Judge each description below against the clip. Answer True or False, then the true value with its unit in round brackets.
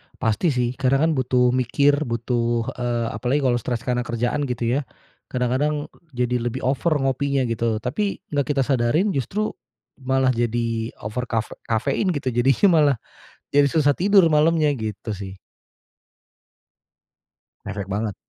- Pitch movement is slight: False (3.4 semitones)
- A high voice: False (125 Hz)